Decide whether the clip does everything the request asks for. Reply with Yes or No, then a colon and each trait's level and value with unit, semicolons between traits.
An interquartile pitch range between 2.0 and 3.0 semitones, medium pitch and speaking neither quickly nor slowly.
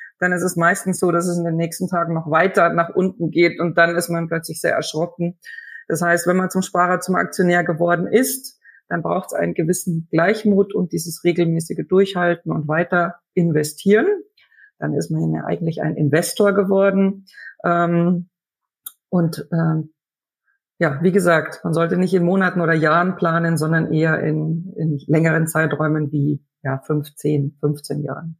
Yes: narrow, 2.5 semitones; medium, 170 Hz; average, 165 wpm